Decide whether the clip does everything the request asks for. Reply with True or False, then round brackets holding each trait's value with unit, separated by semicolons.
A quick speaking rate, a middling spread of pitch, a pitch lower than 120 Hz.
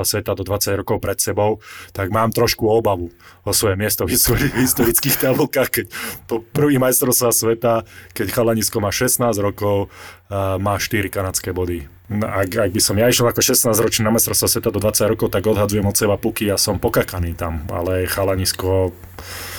True (185 wpm; 3.3 semitones; 105 Hz)